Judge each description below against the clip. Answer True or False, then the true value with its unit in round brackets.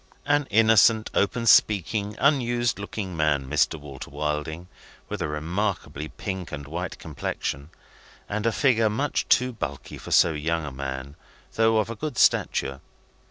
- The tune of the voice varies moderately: False (7.0 semitones)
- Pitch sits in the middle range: False (95 Hz)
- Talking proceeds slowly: False (150 wpm)